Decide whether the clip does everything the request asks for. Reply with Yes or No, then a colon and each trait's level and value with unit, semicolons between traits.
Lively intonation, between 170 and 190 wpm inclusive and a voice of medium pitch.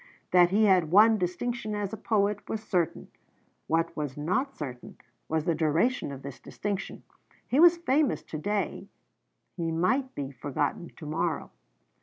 No: wide, 5.7 semitones; average, 155 wpm; medium, 180 Hz